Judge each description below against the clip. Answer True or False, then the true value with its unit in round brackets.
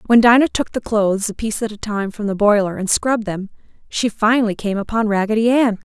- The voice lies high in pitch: True (215 Hz)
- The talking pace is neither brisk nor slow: False (225 wpm)